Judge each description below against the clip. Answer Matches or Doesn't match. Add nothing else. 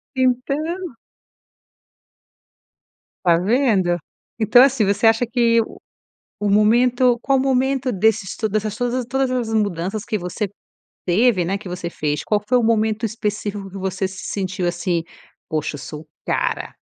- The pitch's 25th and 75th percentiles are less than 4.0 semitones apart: Doesn't match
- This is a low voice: Doesn't match